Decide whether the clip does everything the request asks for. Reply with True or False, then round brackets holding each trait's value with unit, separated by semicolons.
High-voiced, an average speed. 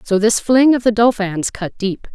False (215 Hz; 225 wpm)